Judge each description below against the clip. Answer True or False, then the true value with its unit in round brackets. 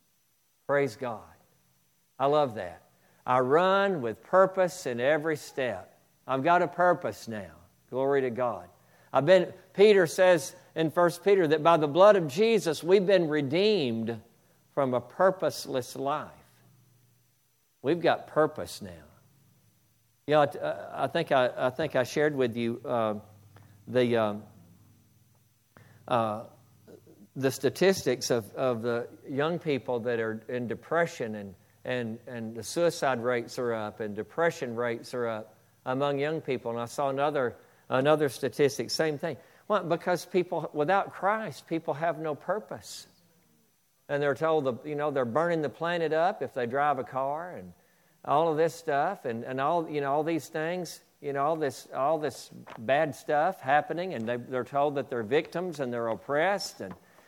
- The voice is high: False (140 Hz)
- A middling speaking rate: True (160 wpm)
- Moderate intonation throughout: False (5.9 semitones)